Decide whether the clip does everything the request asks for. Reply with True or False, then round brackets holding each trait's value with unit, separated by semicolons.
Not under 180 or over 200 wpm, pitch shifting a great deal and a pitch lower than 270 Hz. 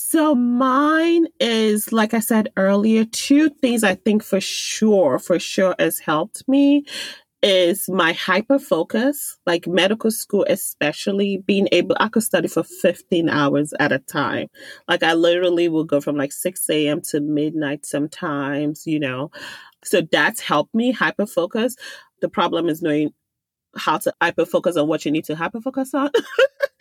False (165 wpm; 6.6 semitones; 190 Hz)